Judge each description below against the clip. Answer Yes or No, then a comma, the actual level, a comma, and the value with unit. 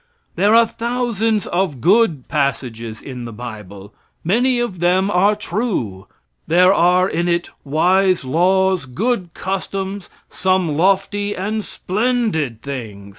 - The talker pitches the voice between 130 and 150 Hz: No, medium, 185 Hz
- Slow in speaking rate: Yes, slow, 125 wpm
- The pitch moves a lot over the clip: Yes, wide, 6.7 semitones